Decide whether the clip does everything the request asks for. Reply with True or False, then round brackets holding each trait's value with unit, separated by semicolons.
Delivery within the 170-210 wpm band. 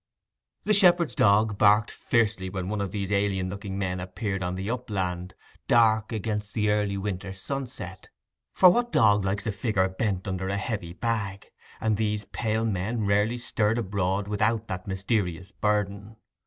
False (155 wpm)